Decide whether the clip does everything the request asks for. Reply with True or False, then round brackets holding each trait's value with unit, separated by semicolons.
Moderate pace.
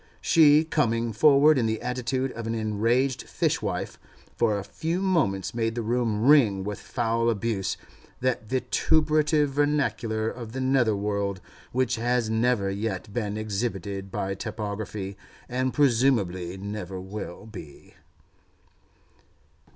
False (125 wpm)